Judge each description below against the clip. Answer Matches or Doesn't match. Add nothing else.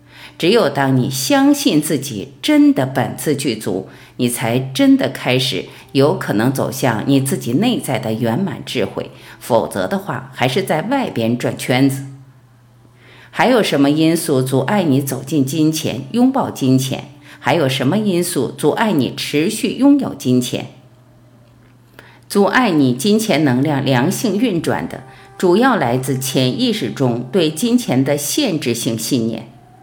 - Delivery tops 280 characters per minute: Doesn't match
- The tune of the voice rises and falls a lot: Doesn't match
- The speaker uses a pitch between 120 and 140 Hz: Matches